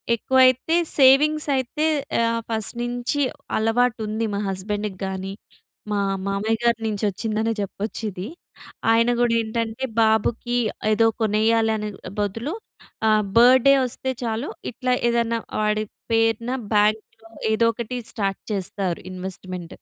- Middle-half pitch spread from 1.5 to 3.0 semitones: Yes, narrow, 2.5 semitones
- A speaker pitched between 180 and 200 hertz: No, high, 225 Hz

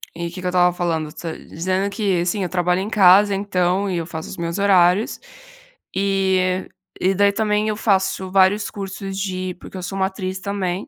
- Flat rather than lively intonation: Yes, narrow, 1.8 semitones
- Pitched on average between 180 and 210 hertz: Yes, high, 190 Hz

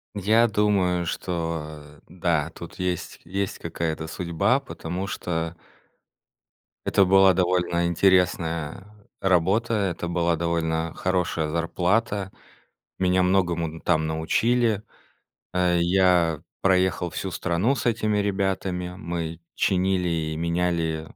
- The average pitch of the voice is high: No, very low, 90 Hz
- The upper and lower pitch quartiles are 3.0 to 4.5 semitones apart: No, narrow, 2.5 semitones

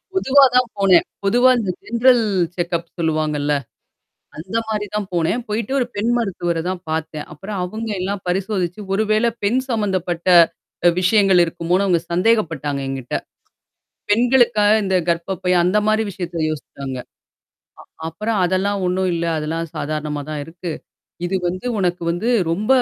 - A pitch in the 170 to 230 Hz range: Yes, medium, 185 Hz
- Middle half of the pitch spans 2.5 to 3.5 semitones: No, average, 4.3 semitones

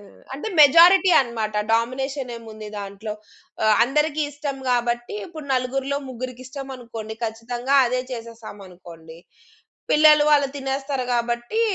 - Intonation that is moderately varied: Yes, average, 3.6 semitones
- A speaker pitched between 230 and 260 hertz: Yes, very high, 250 Hz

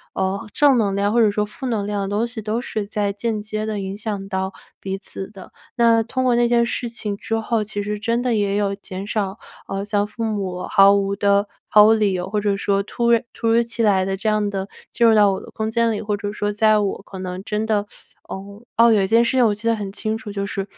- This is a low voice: No, high, 210 Hz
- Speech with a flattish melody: Yes, narrow, 2.1 semitones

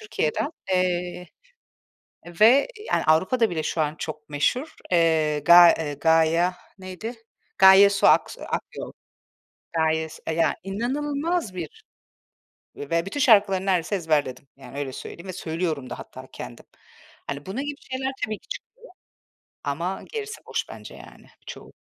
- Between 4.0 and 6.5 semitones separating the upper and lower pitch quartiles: Yes, average, 5.0 semitones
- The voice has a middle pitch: Yes, medium, 175 Hz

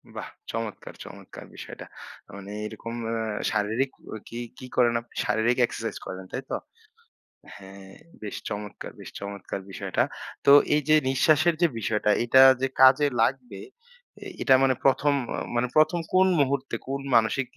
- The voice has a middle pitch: No, low, 120 Hz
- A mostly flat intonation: No, average, 4.2 semitones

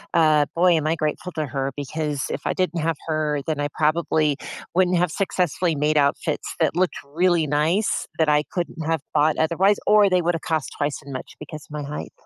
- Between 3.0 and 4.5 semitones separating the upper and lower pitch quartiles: No, narrow, 2.6 semitones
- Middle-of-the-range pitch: Yes, medium, 155 Hz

